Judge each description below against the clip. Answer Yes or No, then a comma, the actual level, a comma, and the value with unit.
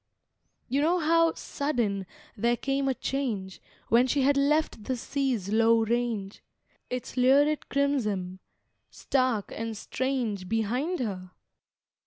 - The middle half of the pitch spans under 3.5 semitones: No, average, 4.5 semitones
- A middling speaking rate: No, slow, 120 wpm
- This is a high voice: Yes, high, 245 Hz